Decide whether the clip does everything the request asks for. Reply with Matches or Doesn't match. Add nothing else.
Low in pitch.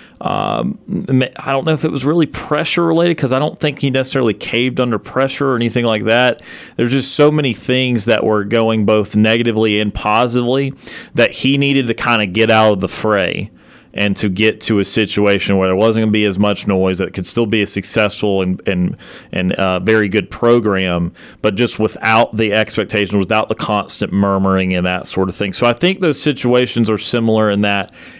Matches